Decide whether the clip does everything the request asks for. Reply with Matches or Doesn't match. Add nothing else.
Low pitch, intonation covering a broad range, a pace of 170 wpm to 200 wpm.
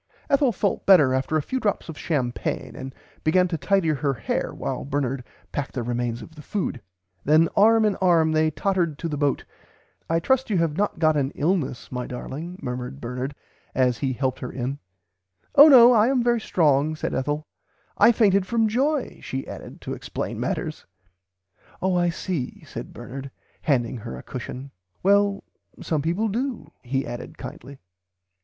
Doesn't match